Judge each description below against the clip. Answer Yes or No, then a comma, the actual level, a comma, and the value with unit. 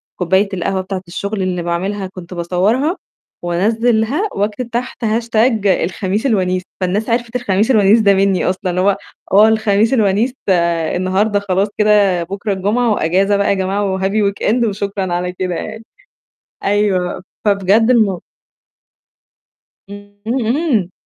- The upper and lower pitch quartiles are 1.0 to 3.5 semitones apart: Yes, average, 2.8 semitones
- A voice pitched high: Yes, high, 200 Hz